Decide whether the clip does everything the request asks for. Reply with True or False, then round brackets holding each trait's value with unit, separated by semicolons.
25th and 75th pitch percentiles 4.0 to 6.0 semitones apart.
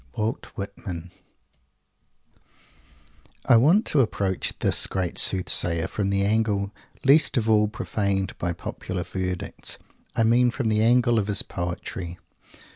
False (3.5 semitones)